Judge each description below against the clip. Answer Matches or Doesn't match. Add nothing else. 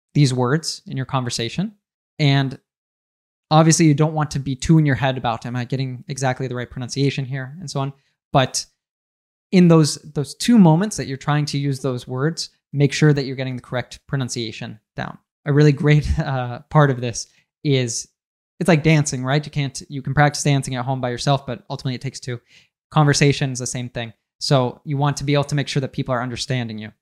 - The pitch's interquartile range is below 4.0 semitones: Matches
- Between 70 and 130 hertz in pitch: Doesn't match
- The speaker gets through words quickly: Matches